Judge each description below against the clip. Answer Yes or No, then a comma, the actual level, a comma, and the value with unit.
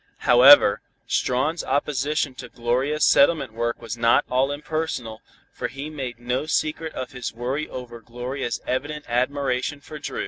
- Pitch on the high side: No, low, 130 Hz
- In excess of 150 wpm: No, average, 145 wpm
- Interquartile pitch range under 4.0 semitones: Yes, average, 3.3 semitones